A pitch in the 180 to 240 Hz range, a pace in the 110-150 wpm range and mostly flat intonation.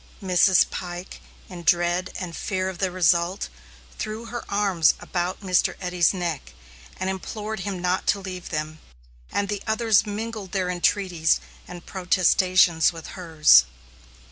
Yes: medium, 185 Hz; average, 140 wpm; narrow, 2.2 semitones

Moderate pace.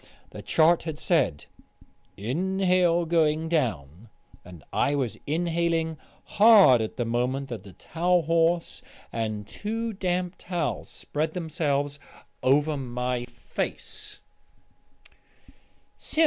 No: slow, 105 wpm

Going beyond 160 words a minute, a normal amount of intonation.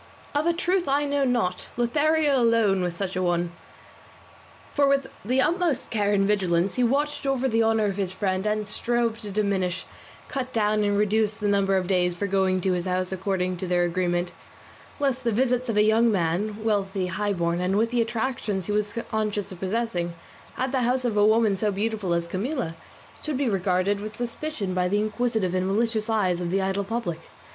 Yes: average, 200 wpm; average, 4.2 semitones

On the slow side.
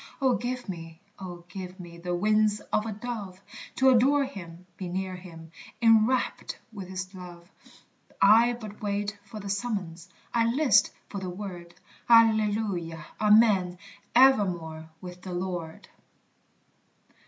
Yes: slow, 130 wpm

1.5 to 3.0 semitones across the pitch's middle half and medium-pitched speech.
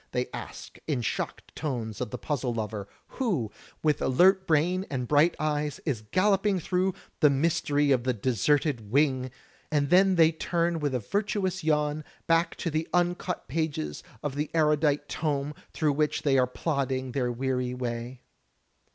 No: average, 4.4 semitones; medium, 145 Hz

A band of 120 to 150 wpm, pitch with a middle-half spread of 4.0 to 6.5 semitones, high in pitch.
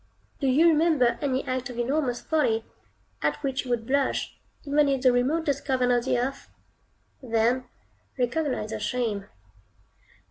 No: average, 145 wpm; narrow, 2.6 semitones; very high, 255 Hz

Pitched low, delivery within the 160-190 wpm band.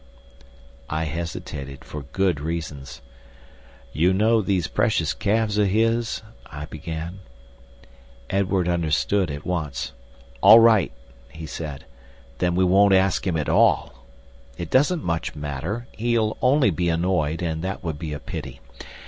No: very low, 85 Hz; slow, 135 wpm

